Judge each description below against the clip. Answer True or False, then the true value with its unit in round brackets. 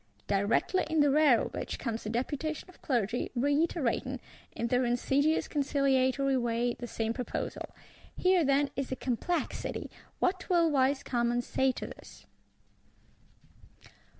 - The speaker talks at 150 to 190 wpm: False (135 wpm)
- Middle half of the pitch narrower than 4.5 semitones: True (3.5 semitones)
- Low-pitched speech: False (265 Hz)